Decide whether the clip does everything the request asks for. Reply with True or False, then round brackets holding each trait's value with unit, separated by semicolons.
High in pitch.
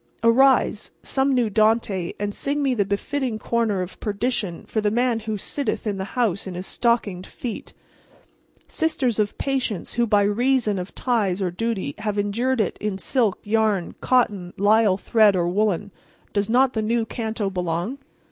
True (215 Hz)